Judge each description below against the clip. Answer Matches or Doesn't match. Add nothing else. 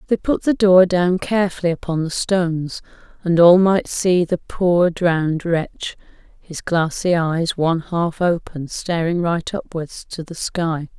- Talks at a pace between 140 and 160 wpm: Matches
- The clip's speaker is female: Matches